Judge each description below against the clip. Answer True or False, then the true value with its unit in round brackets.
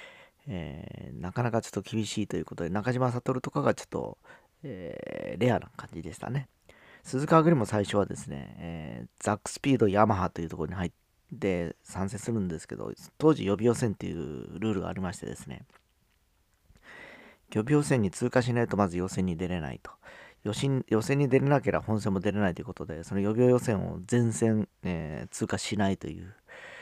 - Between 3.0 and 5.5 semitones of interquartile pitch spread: True (5.1 semitones)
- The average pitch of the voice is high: False (105 Hz)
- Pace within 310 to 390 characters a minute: True (370 characters per minute)